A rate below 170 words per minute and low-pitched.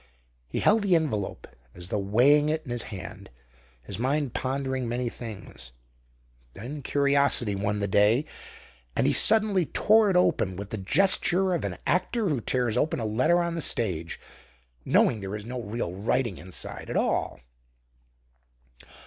Yes: average, 155 wpm; low, 125 Hz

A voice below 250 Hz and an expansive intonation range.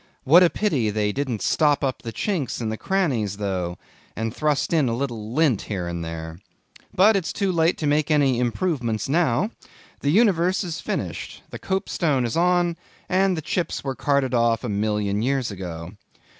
Yes: low, 135 Hz; wide, 7.6 semitones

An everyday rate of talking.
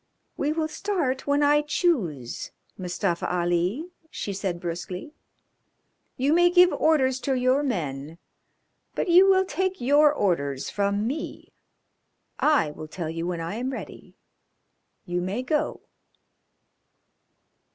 No: slow, 125 wpm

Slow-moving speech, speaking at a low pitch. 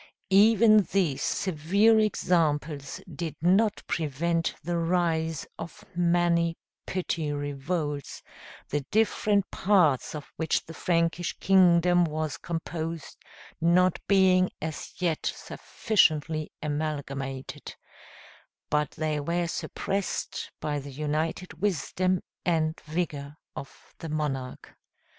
No: slow, 100 wpm; medium, 165 Hz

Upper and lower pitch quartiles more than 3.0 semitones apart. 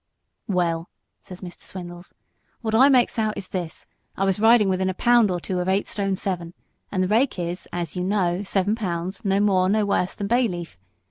No: average, 2.7 semitones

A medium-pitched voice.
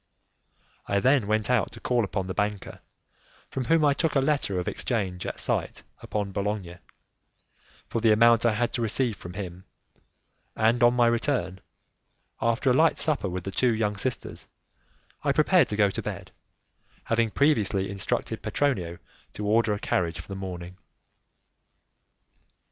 No: low, 110 Hz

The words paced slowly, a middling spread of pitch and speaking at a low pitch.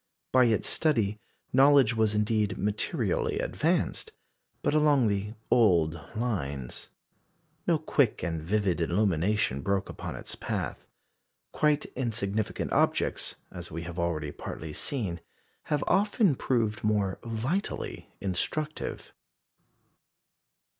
No: slow, 105 wpm; wide, 6.1 semitones; low, 105 Hz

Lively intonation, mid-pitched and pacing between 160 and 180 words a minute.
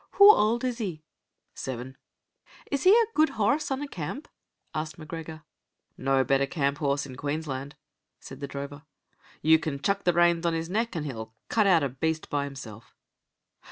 Yes: wide, 6.1 semitones; medium, 155 Hz; average, 175 wpm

